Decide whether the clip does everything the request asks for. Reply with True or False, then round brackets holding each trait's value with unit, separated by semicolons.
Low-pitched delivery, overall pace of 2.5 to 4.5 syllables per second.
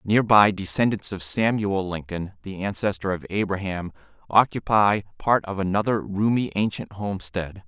False (100 Hz; 4.8 syllables/s)